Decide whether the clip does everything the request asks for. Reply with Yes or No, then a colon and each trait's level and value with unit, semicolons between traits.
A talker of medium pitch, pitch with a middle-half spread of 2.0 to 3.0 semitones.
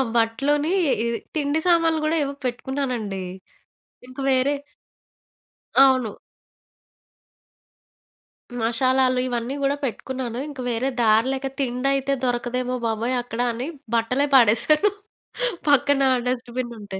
No: very high, 255 Hz; average, 2.7 semitones